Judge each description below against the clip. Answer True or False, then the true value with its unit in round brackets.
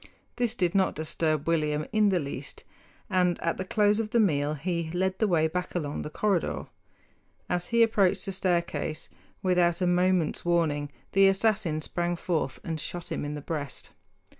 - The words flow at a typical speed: True (175 wpm)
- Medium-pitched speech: True (175 Hz)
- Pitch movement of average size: True (3.5 semitones)